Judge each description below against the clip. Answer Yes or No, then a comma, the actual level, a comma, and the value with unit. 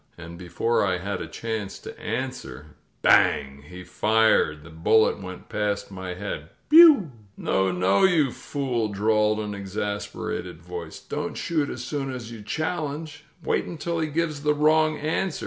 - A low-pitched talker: Yes, low, 110 Hz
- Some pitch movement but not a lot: No, wide, 8.2 semitones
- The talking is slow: No, average, 155 wpm